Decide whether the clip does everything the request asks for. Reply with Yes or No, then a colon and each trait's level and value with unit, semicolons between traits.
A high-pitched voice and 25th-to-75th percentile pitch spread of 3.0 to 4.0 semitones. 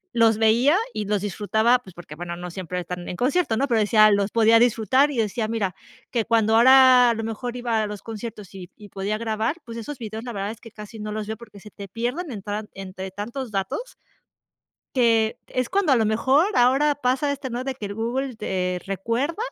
Yes: high, 225 Hz; average, 3.3 semitones